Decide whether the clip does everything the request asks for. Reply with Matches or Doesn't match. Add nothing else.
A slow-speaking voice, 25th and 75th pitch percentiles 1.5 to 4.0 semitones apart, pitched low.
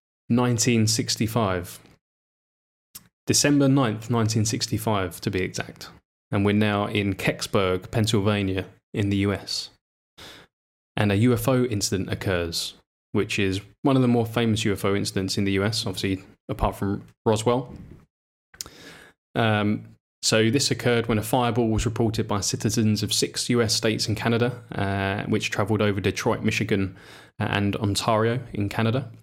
Matches